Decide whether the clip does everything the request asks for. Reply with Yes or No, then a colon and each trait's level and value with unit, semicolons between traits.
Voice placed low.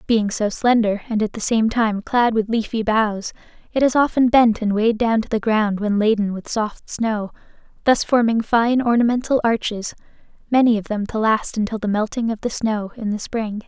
No: high, 220 Hz